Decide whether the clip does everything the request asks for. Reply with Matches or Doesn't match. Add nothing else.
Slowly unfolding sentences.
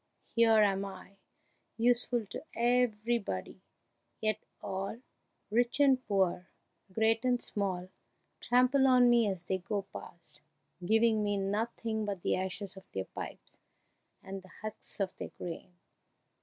Matches